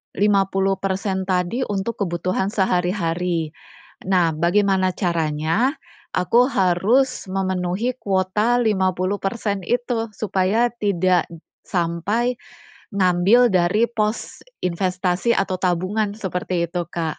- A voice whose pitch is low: No, high, 190 Hz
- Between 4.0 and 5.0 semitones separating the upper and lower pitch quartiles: No, average, 2.9 semitones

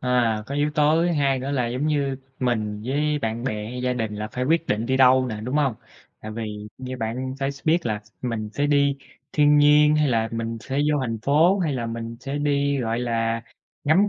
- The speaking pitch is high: No, low, 130 Hz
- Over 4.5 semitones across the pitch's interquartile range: No, average, 4.2 semitones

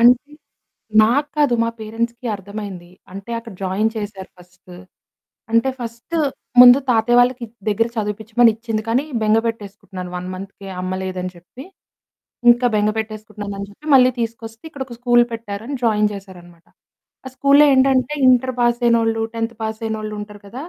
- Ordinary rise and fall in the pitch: Yes, average, 3.0 semitones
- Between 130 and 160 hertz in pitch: No, high, 225 Hz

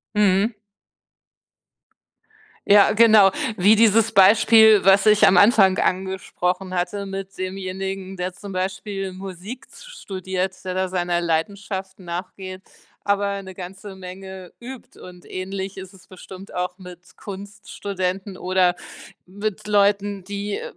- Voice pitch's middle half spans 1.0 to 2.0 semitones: Yes, narrow, 1.5 semitones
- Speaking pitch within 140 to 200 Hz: Yes, high, 190 Hz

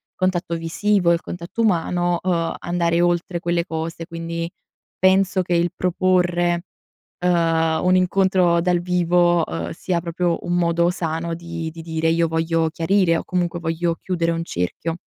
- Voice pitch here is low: No, medium, 170 Hz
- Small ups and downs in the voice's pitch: Yes, narrow, 1.2 semitones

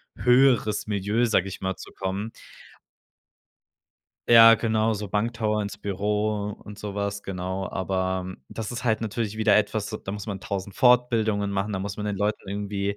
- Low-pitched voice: Yes, low, 105 Hz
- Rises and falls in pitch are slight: Yes, narrow, 1.8 semitones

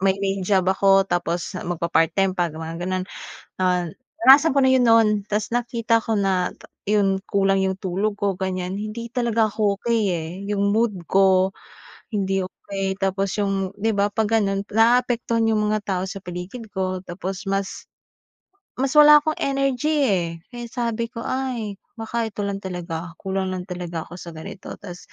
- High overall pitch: Yes, high, 195 Hz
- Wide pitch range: No, average, 3.4 semitones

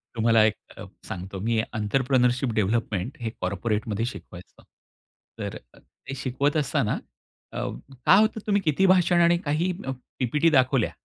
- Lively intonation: Yes, wide, 5.7 semitones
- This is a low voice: Yes, low, 125 Hz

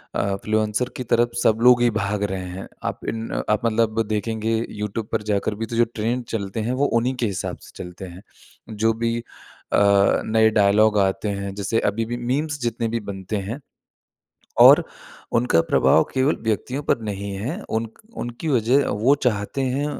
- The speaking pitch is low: Yes, low, 115 Hz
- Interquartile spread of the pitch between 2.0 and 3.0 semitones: Yes, average, 2.7 semitones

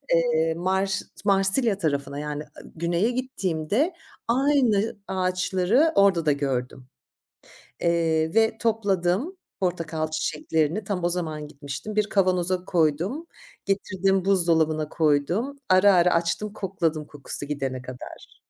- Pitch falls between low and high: Yes, medium, 180 Hz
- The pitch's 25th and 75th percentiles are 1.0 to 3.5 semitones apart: No, average, 4.2 semitones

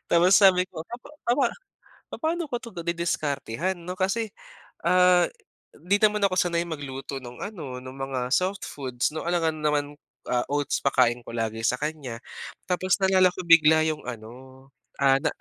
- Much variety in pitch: Yes, wide, 5.7 semitones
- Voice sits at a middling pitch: Yes, medium, 160 Hz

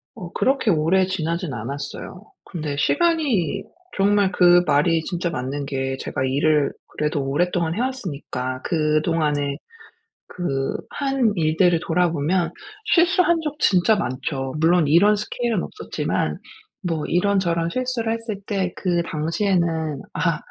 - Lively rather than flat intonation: No, average, 4.9 semitones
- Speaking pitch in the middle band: Yes, medium, 170 Hz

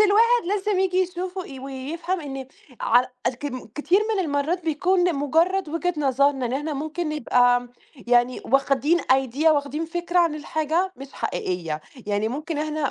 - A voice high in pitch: Yes, very high, 300 Hz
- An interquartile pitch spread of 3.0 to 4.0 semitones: No, average, 4.7 semitones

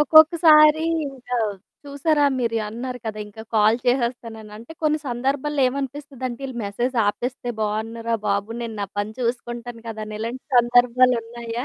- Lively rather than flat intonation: No, average, 2.9 semitones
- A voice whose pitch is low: No, high, 240 Hz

